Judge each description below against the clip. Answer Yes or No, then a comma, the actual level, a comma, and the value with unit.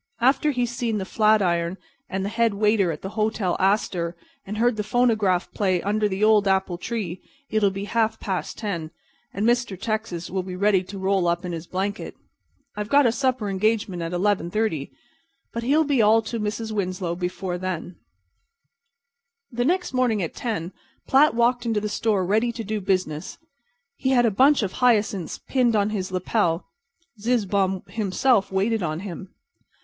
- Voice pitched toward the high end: Yes, high, 205 Hz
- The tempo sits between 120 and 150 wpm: No, average, 175 wpm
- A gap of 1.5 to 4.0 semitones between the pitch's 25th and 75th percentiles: Yes, average, 3.5 semitones